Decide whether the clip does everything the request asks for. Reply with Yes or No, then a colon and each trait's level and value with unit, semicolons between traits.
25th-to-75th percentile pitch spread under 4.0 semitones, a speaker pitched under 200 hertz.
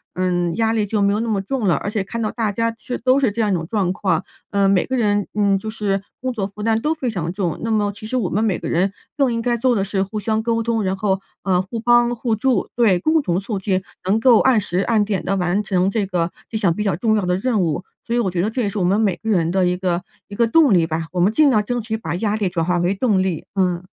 No: average, 3.4 semitones; high, 205 Hz